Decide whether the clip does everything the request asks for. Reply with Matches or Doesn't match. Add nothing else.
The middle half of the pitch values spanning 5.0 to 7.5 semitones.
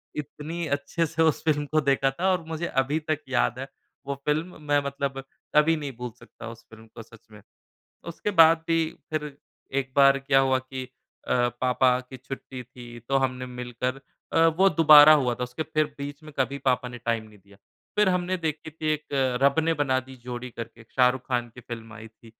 Doesn't match